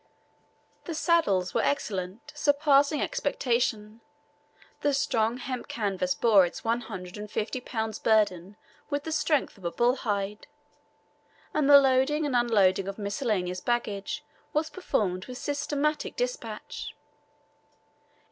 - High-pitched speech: Yes, high, 235 Hz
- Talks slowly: Yes, slow, 120 wpm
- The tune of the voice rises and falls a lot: Yes, wide, 6.1 semitones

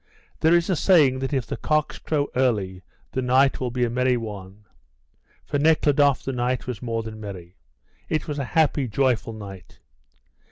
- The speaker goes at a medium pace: Yes, average, 175 wpm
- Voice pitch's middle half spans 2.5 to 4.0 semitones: No, average, 4.6 semitones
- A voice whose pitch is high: No, low, 125 Hz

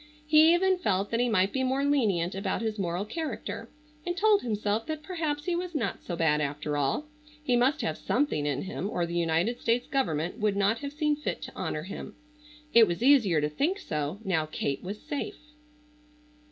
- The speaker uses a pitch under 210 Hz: No, high, 220 Hz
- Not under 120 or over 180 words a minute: No, average, 195 wpm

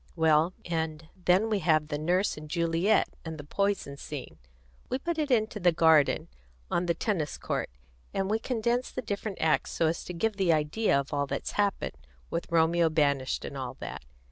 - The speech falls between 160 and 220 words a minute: Yes, average, 190 wpm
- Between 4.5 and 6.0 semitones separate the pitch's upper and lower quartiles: Yes, average, 4.9 semitones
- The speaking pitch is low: No, medium, 170 Hz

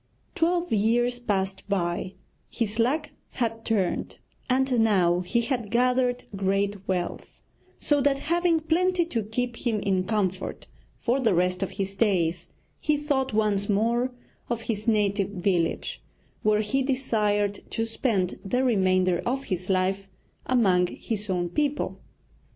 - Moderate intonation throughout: Yes, average, 4.6 semitones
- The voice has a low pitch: No, high, 215 Hz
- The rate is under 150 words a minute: Yes, average, 140 wpm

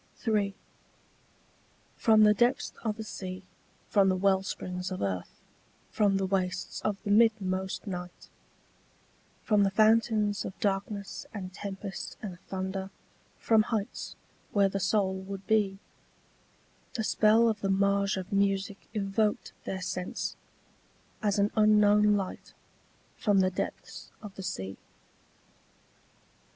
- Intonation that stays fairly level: Yes, narrow, 1.8 semitones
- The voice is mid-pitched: No, high, 200 Hz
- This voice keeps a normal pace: No, slow, 125 wpm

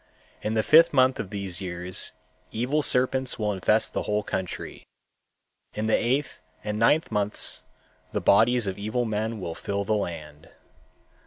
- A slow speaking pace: No, average, 155 wpm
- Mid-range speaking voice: No, low, 105 Hz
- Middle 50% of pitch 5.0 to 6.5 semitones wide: No, average, 3.9 semitones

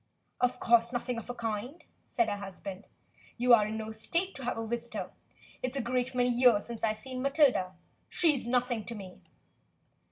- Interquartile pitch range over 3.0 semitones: No, narrow, 2.6 semitones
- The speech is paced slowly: No, average, 185 wpm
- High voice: Yes, high, 235 Hz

